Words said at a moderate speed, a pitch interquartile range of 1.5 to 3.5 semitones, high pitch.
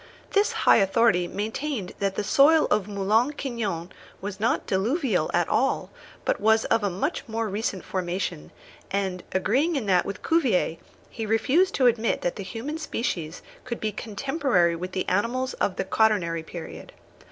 No: average, 160 wpm; average, 5.2 semitones; high, 215 Hz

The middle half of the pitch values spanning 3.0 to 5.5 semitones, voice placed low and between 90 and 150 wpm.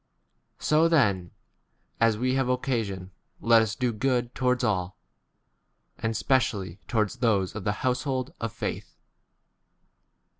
Yes: average, 3.8 semitones; low, 115 Hz; slow, 135 wpm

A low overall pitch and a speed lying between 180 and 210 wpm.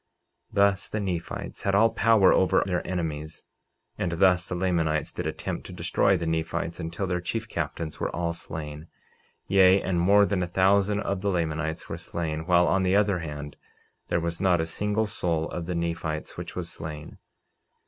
Yes: very low, 90 Hz; average, 185 wpm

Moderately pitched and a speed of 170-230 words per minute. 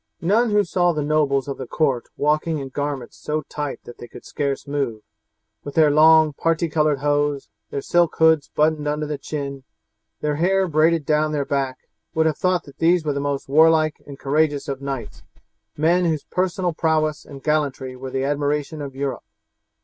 Yes: medium, 150 Hz; average, 185 wpm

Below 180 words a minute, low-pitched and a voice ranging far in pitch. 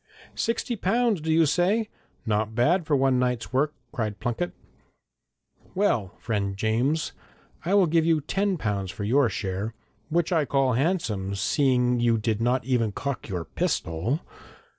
Yes: average, 150 wpm; low, 130 Hz; wide, 6.8 semitones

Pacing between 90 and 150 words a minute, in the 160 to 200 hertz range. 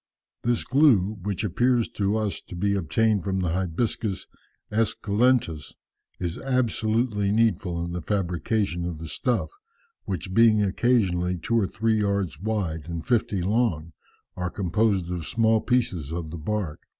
No: average, 145 wpm; low, 100 Hz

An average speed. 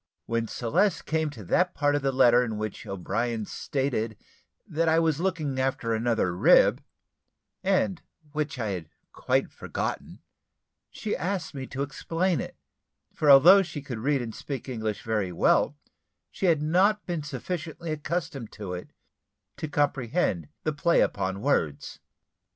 Yes: average, 150 wpm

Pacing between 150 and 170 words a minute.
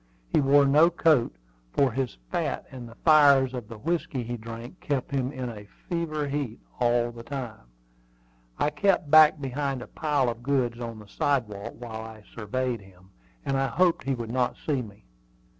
No: average, 180 wpm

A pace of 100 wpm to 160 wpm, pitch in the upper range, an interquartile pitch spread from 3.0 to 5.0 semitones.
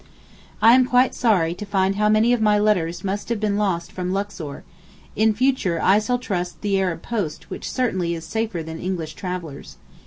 No: average, 190 wpm; high, 200 Hz; average, 3.8 semitones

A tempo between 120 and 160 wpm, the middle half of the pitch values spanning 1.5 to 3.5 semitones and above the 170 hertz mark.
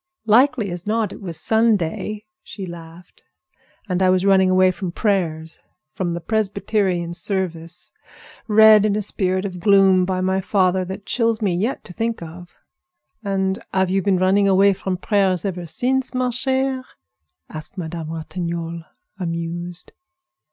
Yes: average, 150 wpm; average, 3.0 semitones; high, 190 Hz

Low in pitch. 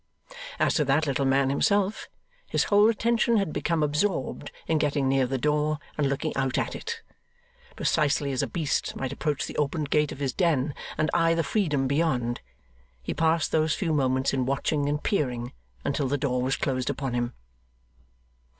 No: medium, 145 Hz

